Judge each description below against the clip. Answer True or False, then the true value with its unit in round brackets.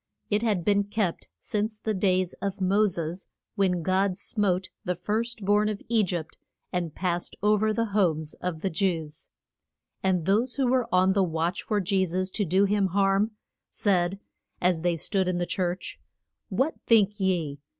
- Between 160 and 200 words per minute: True (175 wpm)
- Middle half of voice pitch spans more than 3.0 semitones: False (2.7 semitones)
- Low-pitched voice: False (190 Hz)